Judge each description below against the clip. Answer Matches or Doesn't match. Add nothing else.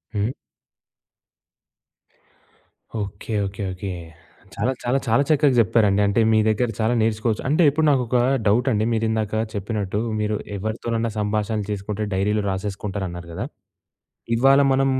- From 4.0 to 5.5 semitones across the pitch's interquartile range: Doesn't match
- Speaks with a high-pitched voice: Doesn't match